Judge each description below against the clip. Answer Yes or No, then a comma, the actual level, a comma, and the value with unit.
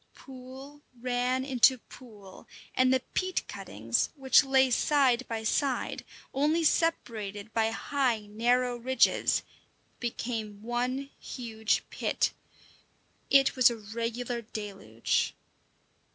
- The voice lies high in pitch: Yes, high, 245 Hz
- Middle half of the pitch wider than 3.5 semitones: No, average, 3.0 semitones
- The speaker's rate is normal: No, slow, 105 wpm